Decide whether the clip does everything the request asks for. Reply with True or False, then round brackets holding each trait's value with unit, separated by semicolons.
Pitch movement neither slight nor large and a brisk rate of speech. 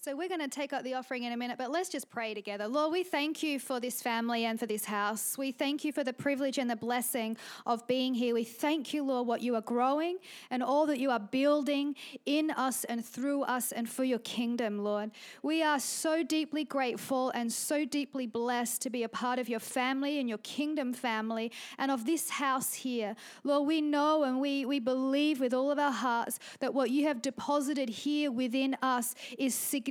True (3.3 semitones; 220 wpm)